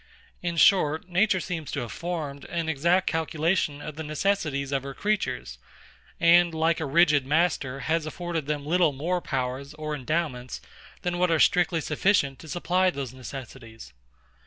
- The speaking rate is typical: Yes, average, 160 wpm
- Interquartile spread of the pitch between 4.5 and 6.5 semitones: No, average, 3.9 semitones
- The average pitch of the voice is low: No, medium, 160 Hz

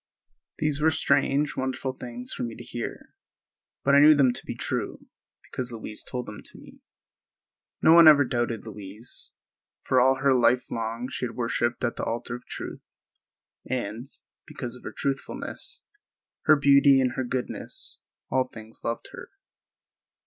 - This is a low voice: Yes, low, 125 Hz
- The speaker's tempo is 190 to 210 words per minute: No, average, 160 wpm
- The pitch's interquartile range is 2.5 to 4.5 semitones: Yes, average, 2.8 semitones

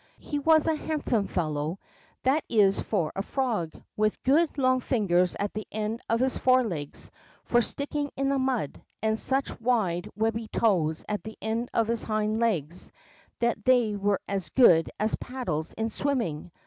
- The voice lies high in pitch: Yes, high, 220 Hz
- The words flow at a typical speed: Yes, average, 165 wpm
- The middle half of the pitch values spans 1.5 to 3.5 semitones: No, average, 4.8 semitones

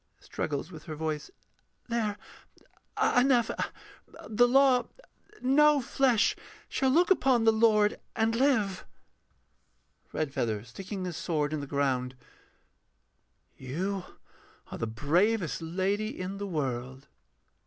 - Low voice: No, high, 195 Hz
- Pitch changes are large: Yes, wide, 7.8 semitones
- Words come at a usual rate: No, slow, 110 wpm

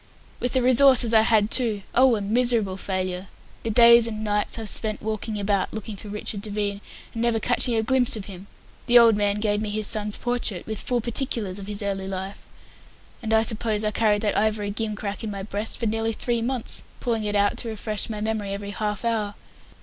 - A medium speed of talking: No, fast, 210 wpm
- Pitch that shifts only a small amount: Yes, narrow, 2.0 semitones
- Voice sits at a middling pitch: No, high, 215 Hz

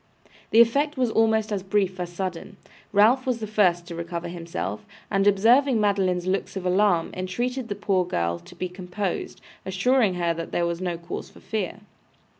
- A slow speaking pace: No, average, 180 wpm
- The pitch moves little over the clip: No, average, 3.6 semitones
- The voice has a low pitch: No, high, 190 Hz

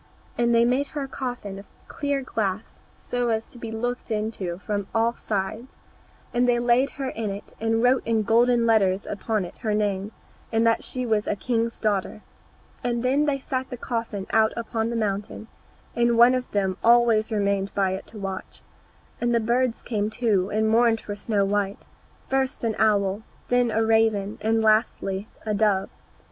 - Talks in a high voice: Yes, high, 225 Hz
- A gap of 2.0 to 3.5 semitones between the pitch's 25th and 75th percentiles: Yes, average, 2.7 semitones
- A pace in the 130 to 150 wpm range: No, average, 180 wpm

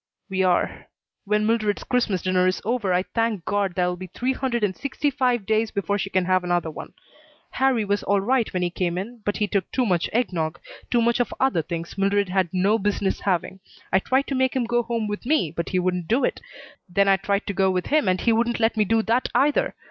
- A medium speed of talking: No, fast, 240 wpm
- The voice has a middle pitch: No, high, 205 Hz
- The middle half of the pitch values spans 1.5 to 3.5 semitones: No, average, 4.3 semitones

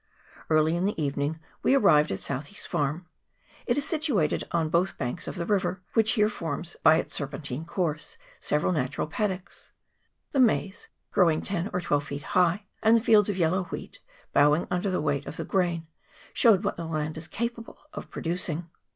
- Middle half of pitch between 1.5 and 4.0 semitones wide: No, average, 4.5 semitones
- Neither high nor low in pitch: Yes, medium, 170 Hz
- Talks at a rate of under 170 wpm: No, average, 180 wpm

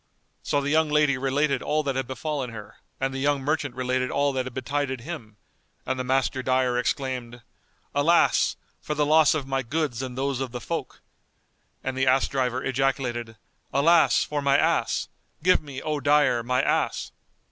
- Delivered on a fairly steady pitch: Yes, narrow, 2.2 semitones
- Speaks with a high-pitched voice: No, low, 135 Hz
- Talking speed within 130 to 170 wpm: No, average, 180 wpm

